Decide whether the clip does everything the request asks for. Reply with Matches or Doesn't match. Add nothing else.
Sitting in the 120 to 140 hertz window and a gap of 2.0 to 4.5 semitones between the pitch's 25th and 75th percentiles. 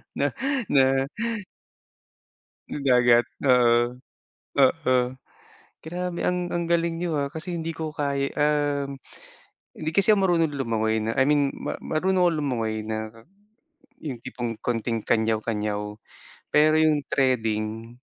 Doesn't match